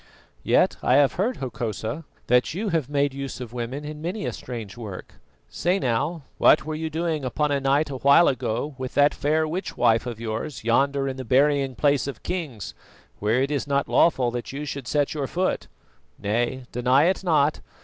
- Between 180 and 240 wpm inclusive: Yes, average, 195 wpm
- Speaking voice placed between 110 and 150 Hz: Yes, medium, 140 Hz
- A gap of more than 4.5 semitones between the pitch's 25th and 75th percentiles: No, average, 3.7 semitones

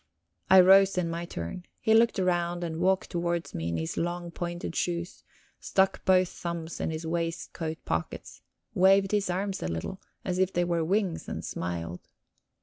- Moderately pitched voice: Yes, medium, 175 Hz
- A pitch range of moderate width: No, narrow, 2.3 semitones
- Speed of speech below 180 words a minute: Yes, average, 170 wpm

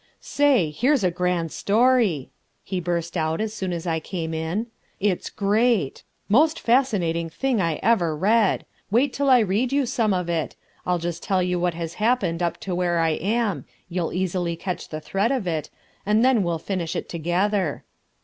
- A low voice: No, medium, 185 Hz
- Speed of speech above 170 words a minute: Yes, average, 180 wpm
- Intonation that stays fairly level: No, average, 4.8 semitones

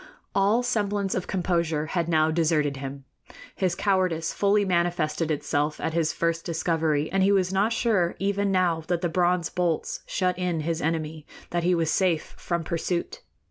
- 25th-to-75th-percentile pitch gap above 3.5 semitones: No, average, 2.8 semitones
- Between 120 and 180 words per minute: Yes, average, 170 wpm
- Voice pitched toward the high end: No, medium, 170 Hz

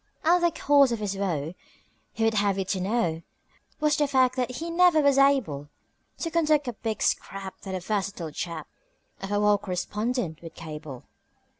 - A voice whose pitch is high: Yes, high, 210 Hz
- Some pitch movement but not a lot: No, wide, 7.3 semitones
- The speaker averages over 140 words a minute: Yes, average, 180 wpm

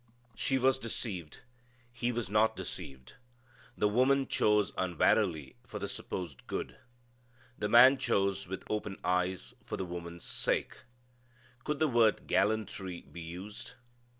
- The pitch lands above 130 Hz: No, low, 105 Hz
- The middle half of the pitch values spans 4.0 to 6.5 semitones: Yes, average, 4.8 semitones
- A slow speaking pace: Yes, slow, 130 wpm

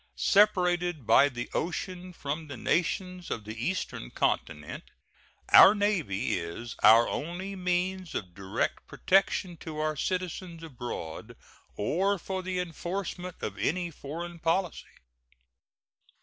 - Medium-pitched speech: Yes, medium, 170 Hz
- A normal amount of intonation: No, wide, 6.2 semitones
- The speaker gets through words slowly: Yes, slow, 120 wpm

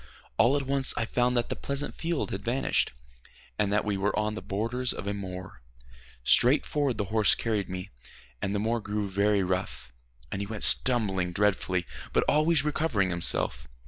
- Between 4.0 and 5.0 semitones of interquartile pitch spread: Yes, average, 4.3 semitones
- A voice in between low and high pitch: No, low, 105 Hz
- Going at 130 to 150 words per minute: No, average, 180 wpm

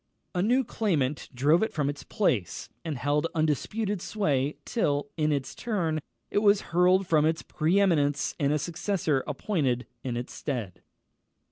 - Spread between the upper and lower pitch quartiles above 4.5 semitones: Yes, average, 5.1 semitones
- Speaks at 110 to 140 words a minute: No, average, 155 wpm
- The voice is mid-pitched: Yes, medium, 155 Hz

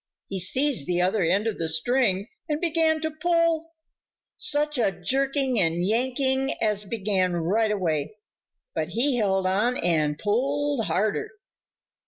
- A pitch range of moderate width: No, wide, 6.9 semitones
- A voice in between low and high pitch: No, high, 220 Hz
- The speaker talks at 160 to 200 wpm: No, average, 140 wpm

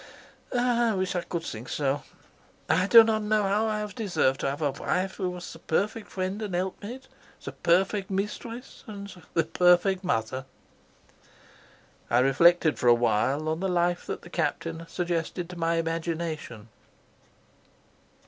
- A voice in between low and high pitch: Yes, medium, 175 Hz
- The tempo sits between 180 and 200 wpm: No, average, 155 wpm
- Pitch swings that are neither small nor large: Yes, average, 4.0 semitones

